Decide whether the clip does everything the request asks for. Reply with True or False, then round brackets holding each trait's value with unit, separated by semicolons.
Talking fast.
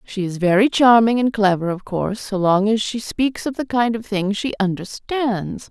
True (210 wpm)